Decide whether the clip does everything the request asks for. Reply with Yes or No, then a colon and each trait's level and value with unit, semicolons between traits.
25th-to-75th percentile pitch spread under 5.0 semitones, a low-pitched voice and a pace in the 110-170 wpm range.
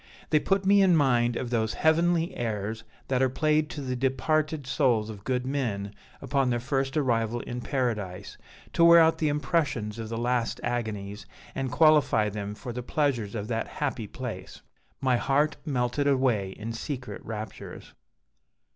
Yes: average, 4.5 semitones; low, 125 Hz; average, 165 wpm